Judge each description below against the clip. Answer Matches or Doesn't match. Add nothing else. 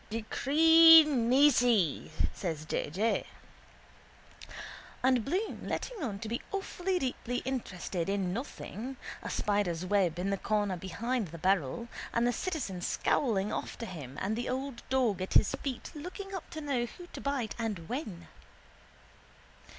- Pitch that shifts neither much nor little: Doesn't match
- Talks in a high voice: Matches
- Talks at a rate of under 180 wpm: Matches